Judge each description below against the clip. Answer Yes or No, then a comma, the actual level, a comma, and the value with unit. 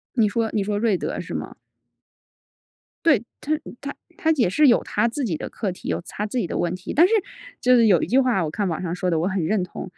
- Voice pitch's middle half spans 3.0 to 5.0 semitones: No, wide, 5.4 semitones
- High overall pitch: Yes, high, 210 Hz